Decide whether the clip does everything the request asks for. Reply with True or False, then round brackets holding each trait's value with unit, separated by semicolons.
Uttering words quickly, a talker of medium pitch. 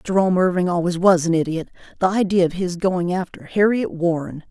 False (185 wpm; 180 Hz)